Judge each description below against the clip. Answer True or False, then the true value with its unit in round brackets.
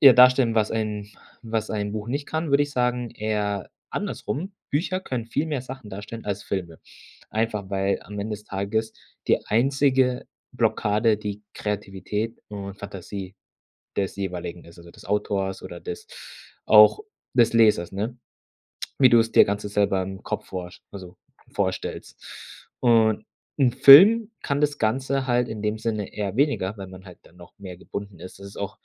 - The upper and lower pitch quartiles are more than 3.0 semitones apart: True (3.9 semitones)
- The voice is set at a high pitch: False (105 Hz)